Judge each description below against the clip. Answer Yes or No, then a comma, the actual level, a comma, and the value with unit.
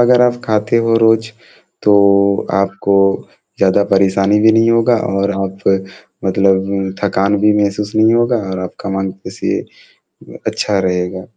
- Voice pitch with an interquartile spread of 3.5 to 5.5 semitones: No, narrow, 2.6 semitones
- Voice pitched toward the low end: Yes, low, 100 Hz